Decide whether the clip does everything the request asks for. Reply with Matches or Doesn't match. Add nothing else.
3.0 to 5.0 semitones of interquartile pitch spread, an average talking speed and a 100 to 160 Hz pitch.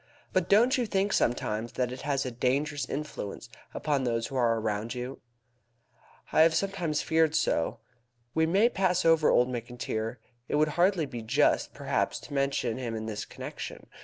Doesn't match